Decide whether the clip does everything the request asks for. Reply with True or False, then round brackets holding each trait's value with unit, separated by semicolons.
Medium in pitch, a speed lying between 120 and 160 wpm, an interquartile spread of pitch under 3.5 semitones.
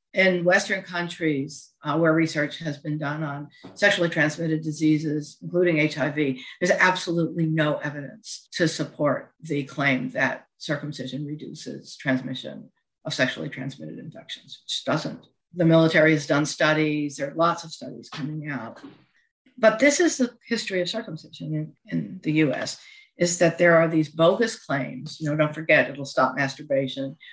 True (155 Hz; 155 wpm; 2.9 semitones)